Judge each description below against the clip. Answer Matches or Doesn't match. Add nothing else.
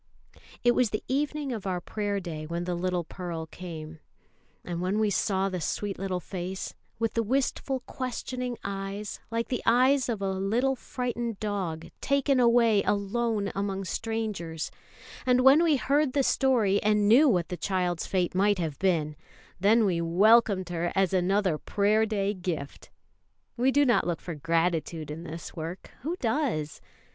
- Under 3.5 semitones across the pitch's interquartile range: Doesn't match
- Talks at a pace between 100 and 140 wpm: Doesn't match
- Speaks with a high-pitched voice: Matches